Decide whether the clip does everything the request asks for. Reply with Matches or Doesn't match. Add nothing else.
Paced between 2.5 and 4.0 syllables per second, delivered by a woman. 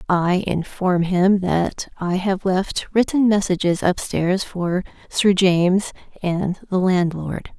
Matches